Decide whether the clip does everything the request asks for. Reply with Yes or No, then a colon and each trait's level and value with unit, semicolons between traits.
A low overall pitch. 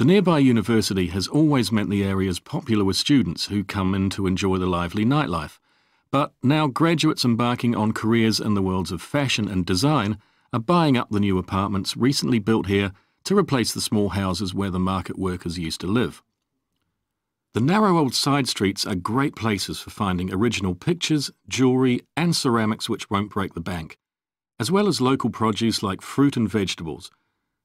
Yes: low, 110 Hz